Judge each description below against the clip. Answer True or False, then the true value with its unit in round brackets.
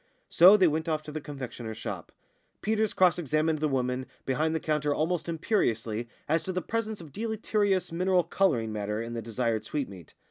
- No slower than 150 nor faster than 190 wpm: True (180 wpm)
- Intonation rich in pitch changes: True (7.0 semitones)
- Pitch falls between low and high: True (155 Hz)